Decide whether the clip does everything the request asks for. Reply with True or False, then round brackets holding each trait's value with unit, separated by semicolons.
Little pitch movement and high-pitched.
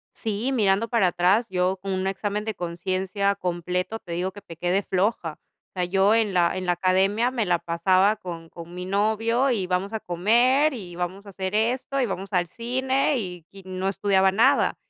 False (3.4 semitones; 195 Hz)